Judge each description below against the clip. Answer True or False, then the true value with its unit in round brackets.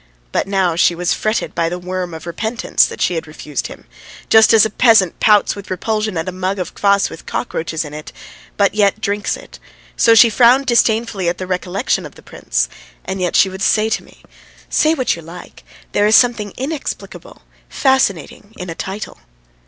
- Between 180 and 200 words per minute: True (195 wpm)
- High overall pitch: True (195 Hz)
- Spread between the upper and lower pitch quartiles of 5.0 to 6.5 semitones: False (3.8 semitones)